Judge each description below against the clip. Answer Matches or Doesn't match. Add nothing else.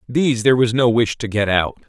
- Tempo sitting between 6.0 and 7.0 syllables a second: Matches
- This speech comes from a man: Matches